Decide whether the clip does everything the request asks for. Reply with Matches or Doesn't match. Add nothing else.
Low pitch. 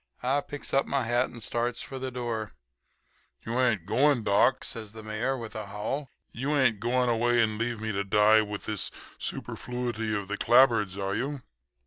Matches